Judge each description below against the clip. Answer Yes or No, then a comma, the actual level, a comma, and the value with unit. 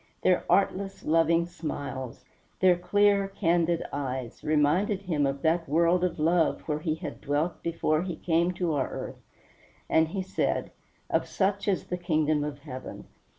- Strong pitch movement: No, average, 3.2 semitones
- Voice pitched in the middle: Yes, medium, 165 Hz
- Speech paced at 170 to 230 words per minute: No, average, 155 wpm